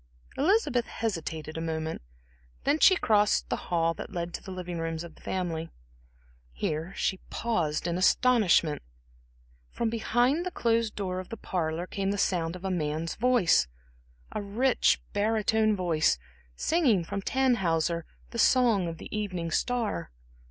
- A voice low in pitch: No, high, 190 Hz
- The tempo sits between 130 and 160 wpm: Yes, average, 150 wpm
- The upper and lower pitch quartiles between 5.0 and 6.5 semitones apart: Yes, wide, 5.6 semitones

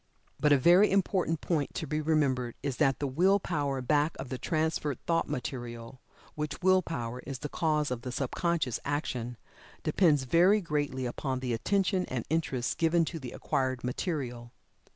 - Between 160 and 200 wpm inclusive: Yes, average, 170 wpm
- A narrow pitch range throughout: No, average, 4.5 semitones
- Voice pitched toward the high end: No, medium, 145 Hz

